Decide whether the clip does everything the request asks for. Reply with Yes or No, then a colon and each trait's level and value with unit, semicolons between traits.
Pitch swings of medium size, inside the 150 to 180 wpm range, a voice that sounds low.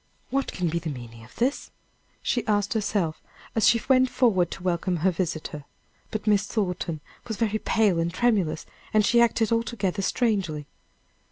No: average, 4.9 semitones; average, 165 wpm; high, 200 Hz